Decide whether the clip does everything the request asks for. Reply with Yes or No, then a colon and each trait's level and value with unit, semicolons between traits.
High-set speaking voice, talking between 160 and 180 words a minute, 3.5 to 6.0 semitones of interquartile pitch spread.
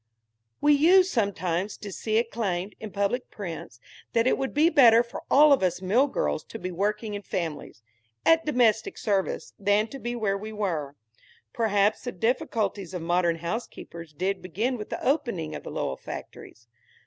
Yes: high, 210 Hz; average, 175 wpm; average, 4.8 semitones